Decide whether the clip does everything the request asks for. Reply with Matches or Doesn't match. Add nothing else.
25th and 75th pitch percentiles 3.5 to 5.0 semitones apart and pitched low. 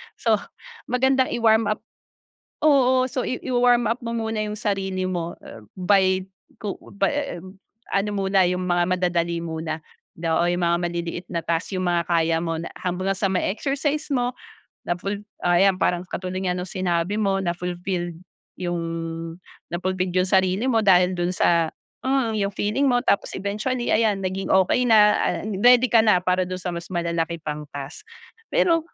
Doesn't match